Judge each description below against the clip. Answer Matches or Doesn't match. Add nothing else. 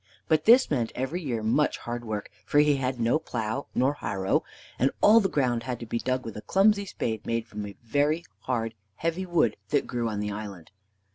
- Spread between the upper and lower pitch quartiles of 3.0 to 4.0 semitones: Doesn't match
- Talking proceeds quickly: Matches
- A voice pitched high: Doesn't match